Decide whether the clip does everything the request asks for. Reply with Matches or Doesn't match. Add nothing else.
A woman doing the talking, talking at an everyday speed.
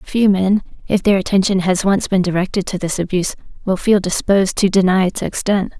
Matches